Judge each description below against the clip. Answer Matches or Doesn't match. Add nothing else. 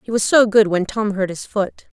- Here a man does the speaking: Doesn't match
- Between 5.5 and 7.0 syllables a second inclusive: Doesn't match